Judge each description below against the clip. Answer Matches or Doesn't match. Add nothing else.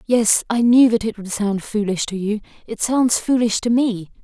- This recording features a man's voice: Doesn't match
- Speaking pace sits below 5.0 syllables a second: Matches